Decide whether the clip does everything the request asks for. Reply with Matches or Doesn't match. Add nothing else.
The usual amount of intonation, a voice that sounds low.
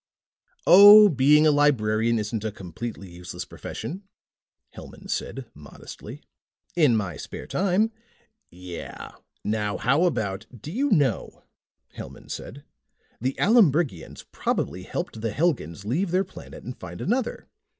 Doesn't match